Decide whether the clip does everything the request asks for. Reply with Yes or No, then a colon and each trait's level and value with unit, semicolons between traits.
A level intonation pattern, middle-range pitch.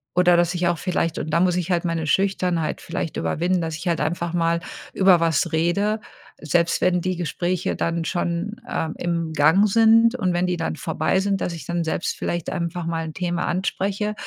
Yes: narrow, 1.8 semitones; medium, 175 Hz